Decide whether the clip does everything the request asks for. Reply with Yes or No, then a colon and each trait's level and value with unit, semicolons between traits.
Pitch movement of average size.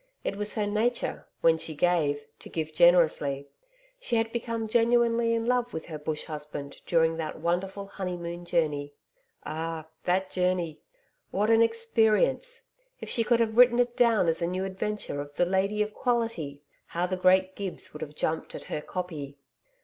No: wide, 5.9 semitones